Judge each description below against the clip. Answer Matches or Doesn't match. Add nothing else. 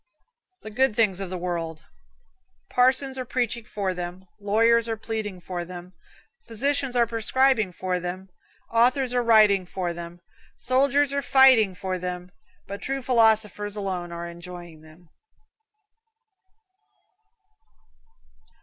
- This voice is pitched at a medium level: Doesn't match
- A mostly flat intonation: Doesn't match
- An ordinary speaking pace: Doesn't match